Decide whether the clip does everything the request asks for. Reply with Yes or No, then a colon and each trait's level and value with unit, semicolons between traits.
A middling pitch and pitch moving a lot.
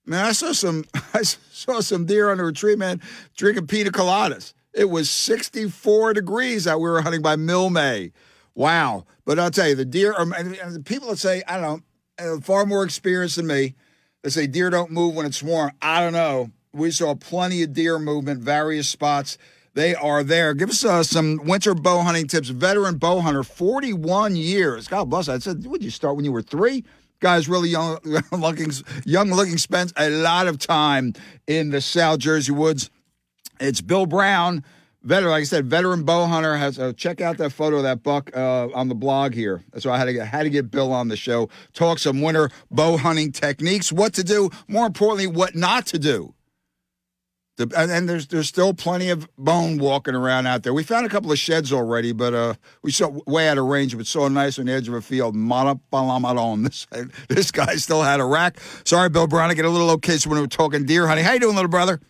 No: medium, 160 Hz; average, 4.3 semitones